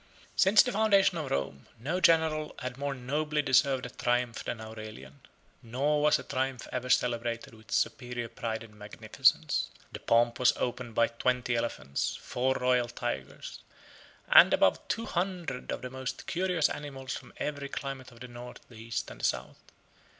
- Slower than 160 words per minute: No, average, 170 wpm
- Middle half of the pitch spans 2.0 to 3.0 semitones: No, average, 3.9 semitones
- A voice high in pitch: No, low, 125 Hz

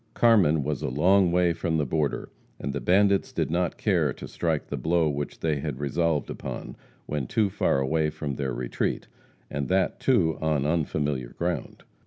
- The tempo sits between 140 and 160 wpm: No, average, 180 wpm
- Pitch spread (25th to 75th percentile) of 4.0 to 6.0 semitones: No, average, 3.4 semitones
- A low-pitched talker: Yes, very low, 80 Hz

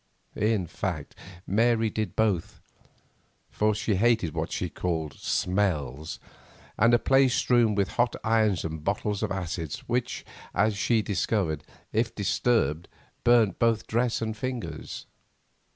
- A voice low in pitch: Yes, low, 105 Hz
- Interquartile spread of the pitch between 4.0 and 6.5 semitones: Yes, average, 4.4 semitones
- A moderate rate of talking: No, slow, 130 wpm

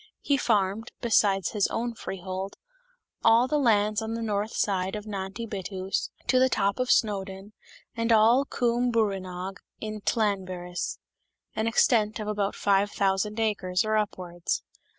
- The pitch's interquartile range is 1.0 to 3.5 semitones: Yes, average, 2.7 semitones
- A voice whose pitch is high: Yes, high, 210 Hz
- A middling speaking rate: Yes, average, 150 wpm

